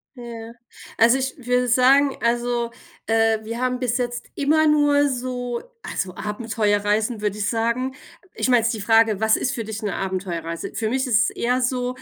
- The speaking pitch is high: Yes, high, 235 Hz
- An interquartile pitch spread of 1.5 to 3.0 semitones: Yes, narrow, 2.5 semitones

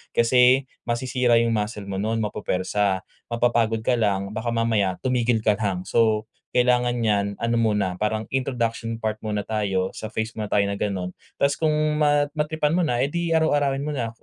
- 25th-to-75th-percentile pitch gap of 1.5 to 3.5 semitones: Yes, average, 3.2 semitones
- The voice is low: Yes, low, 115 Hz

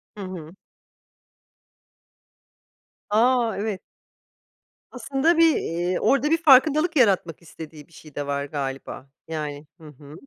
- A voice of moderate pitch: Yes, medium, 180 Hz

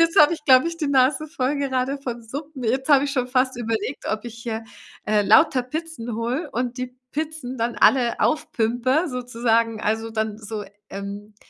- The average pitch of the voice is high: Yes, very high, 250 Hz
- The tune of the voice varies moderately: Yes, average, 3.8 semitones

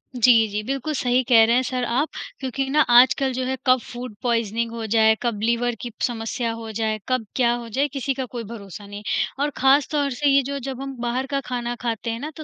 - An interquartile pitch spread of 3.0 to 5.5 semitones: No, narrow, 2.6 semitones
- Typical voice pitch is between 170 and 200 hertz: No, high, 245 Hz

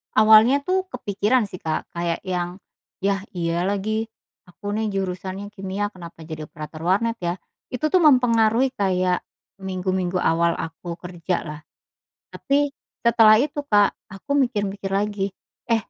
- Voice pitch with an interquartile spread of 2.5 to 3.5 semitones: No, average, 3.9 semitones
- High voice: Yes, high, 195 Hz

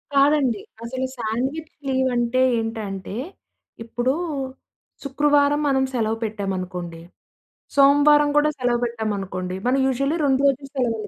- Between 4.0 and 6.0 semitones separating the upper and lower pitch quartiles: Yes, average, 4.3 semitones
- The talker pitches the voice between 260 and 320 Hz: No, very high, 250 Hz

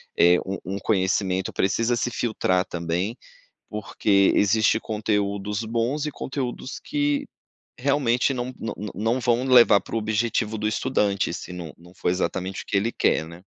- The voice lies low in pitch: Yes, low, 105 Hz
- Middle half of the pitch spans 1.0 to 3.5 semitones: No, average, 4.0 semitones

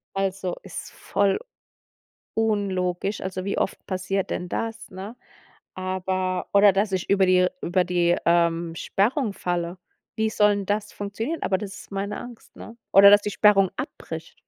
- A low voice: No, high, 195 Hz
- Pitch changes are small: Yes, narrow, 2.0 semitones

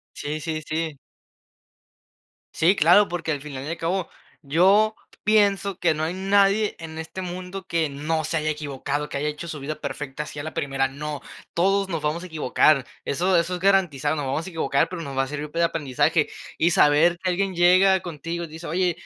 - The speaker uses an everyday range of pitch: Yes, average, 3.5 semitones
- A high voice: No, medium, 165 Hz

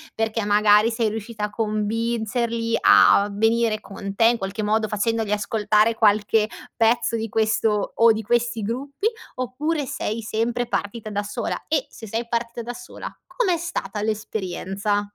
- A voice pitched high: Yes, high, 220 Hz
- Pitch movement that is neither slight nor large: No, narrow, 1.9 semitones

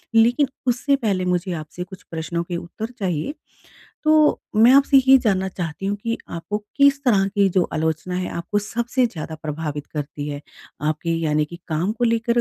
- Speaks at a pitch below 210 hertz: Yes, medium, 185 Hz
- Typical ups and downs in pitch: No, wide, 6.2 semitones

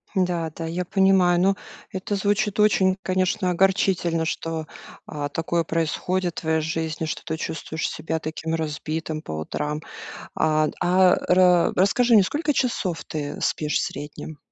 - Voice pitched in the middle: Yes, medium, 170 Hz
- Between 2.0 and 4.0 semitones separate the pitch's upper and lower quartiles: Yes, average, 2.9 semitones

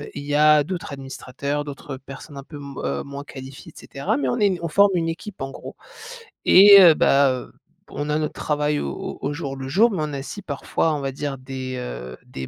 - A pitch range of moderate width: No, narrow, 2.2 semitones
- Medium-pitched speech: Yes, medium, 145 Hz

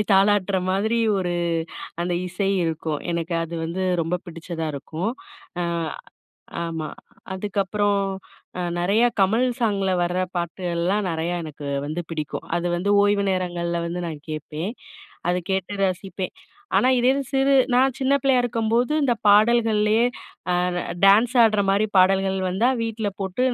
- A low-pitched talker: No, high, 190 Hz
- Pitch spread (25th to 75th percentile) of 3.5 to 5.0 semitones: Yes, average, 3.9 semitones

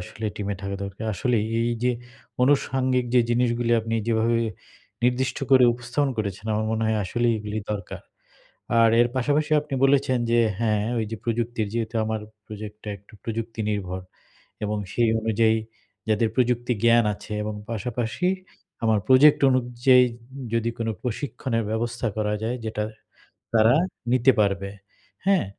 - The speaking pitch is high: No, low, 115 Hz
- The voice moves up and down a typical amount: No, narrow, 2.3 semitones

